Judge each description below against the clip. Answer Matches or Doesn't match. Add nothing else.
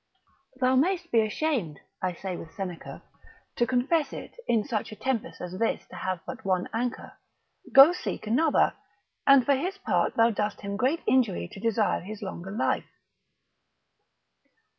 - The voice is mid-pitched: Doesn't match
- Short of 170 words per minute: Matches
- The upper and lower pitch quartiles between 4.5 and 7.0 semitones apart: Matches